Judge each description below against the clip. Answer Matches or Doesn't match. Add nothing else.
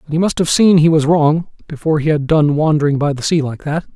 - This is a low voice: Doesn't match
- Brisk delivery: Matches